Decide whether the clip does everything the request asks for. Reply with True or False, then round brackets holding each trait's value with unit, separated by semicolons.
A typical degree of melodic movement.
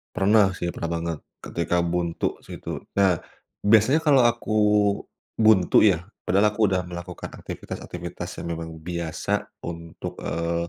True (3.7 semitones)